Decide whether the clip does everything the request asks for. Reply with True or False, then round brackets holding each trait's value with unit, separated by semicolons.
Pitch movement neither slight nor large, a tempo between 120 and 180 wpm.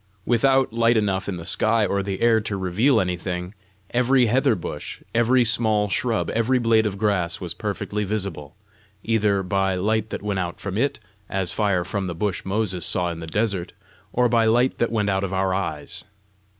False (3.5 semitones; 190 wpm)